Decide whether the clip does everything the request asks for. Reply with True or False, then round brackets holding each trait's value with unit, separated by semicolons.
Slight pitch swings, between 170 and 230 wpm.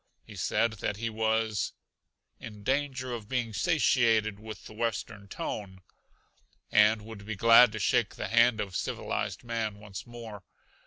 False (1.9 semitones; 150 wpm)